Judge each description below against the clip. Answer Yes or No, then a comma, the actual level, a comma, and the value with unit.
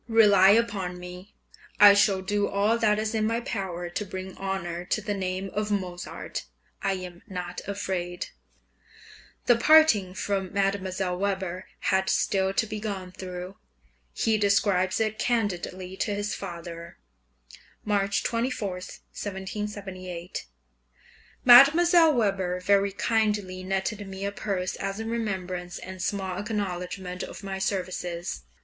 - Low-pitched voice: No, high, 195 Hz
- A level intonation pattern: Yes, narrow, 2.2 semitones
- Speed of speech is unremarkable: No, slow, 130 wpm